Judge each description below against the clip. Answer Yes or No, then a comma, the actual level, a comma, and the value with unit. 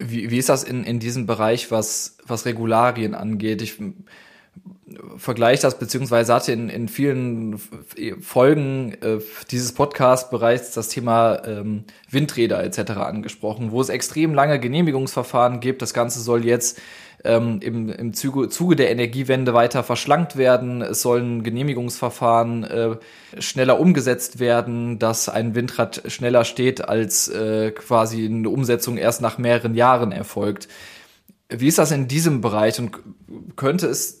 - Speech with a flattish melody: Yes, narrow, 2.2 semitones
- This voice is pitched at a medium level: No, low, 120 Hz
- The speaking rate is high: No, average, 150 wpm